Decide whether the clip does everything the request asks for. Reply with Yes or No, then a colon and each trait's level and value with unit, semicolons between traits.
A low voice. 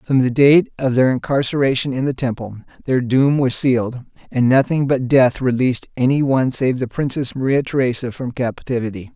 Yes: low, 130 Hz